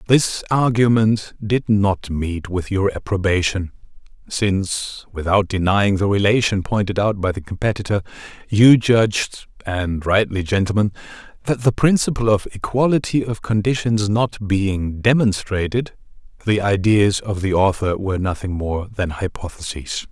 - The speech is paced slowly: Yes, slow, 130 wpm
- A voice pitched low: Yes, low, 100 Hz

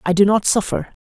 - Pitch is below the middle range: No, high, 195 Hz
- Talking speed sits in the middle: No, fast, 235 wpm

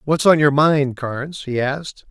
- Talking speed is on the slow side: No, average, 200 wpm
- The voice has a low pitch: No, medium, 145 Hz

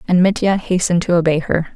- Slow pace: No, fast, 205 wpm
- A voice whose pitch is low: No, medium, 175 Hz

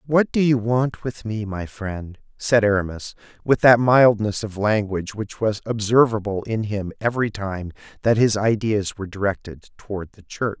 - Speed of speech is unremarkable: Yes, average, 170 wpm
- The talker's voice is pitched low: Yes, low, 105 Hz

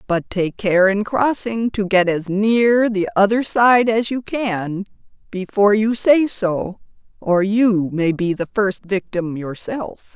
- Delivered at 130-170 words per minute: Yes, average, 160 wpm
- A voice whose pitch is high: Yes, high, 205 Hz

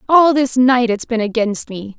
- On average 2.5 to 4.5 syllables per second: Yes, 4.4 syllables/s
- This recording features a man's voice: No, female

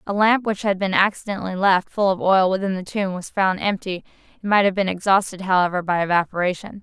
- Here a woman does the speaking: Yes, female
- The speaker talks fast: Yes, fast, 210 wpm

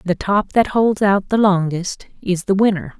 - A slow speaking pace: No, average, 200 wpm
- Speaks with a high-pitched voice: Yes, high, 195 Hz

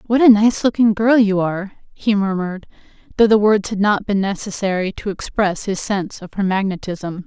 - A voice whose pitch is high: Yes, high, 200 Hz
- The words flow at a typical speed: Yes, average, 190 wpm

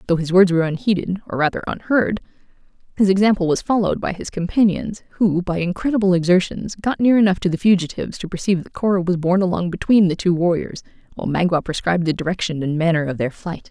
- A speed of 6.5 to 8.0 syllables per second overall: Yes, 6.6 syllables/s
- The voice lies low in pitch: No, medium, 180 Hz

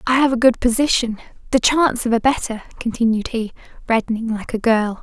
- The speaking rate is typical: Yes, average, 180 wpm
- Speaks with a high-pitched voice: Yes, high, 235 Hz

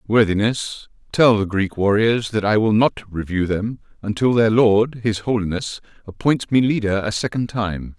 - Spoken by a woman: No, male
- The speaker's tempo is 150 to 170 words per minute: Yes, average, 165 wpm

